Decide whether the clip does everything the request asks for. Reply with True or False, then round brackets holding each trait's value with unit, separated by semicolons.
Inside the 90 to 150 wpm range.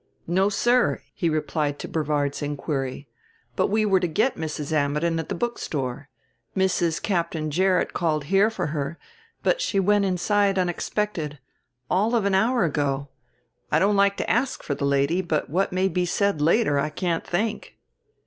False (170 wpm)